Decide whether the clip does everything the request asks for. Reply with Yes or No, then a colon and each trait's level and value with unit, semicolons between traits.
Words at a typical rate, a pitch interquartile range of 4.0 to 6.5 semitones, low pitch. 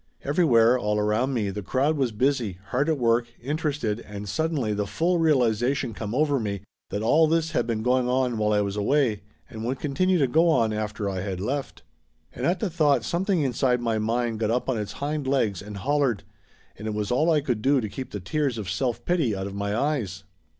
No: fast, 220 wpm; average, 5.3 semitones; low, 120 Hz